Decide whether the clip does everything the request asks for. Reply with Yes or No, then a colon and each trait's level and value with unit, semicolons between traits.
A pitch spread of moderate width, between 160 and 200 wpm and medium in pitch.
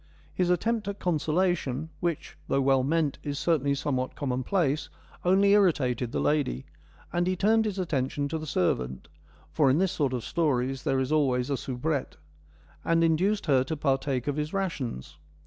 Yes: average, 4.8 semitones; average, 175 wpm; medium, 150 Hz